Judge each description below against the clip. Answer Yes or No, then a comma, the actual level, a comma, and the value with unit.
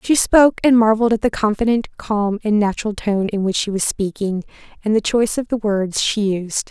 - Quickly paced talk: Yes, fast, 215 wpm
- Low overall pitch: No, high, 215 Hz